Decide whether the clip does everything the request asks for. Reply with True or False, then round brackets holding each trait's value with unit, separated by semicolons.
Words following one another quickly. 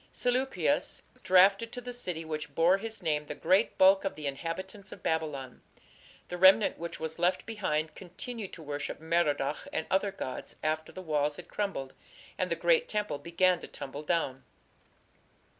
False (170 wpm)